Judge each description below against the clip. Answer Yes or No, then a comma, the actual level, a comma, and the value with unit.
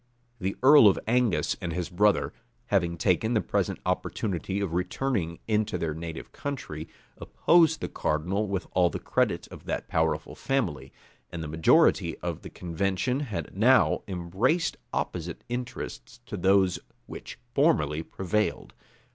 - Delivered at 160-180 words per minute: No, average, 140 wpm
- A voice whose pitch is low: Yes, very low, 95 Hz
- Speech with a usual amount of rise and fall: Yes, average, 5.0 semitones